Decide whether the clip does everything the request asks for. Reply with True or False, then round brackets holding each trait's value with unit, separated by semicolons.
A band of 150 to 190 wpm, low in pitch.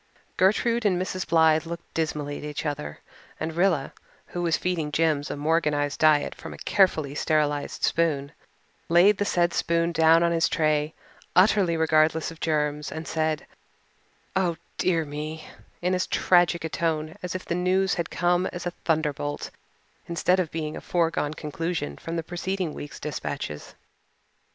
False (160 wpm; 165 Hz)